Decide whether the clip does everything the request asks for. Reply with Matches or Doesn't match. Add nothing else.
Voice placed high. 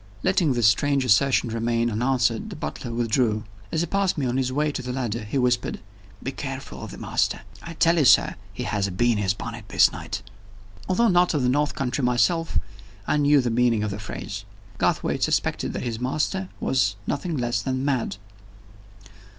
Doesn't match